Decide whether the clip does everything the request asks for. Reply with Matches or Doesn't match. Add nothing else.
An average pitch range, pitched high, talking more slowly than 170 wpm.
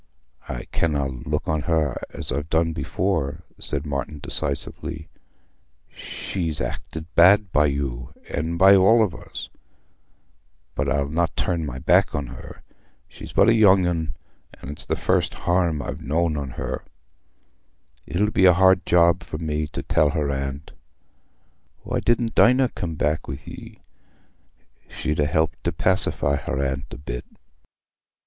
Doesn't match